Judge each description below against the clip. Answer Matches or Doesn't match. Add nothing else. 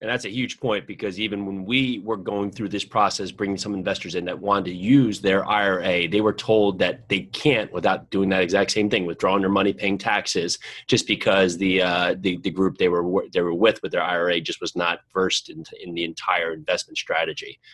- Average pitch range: Doesn't match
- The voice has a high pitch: Doesn't match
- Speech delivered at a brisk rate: Matches